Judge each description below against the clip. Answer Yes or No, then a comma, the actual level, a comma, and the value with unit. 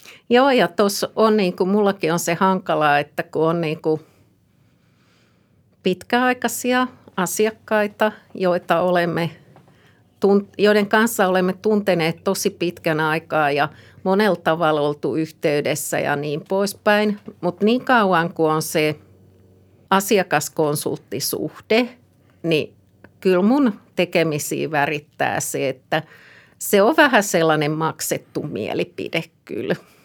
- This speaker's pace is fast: No, average, 110 wpm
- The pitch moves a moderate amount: Yes, average, 4.9 semitones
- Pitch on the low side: No, medium, 175 Hz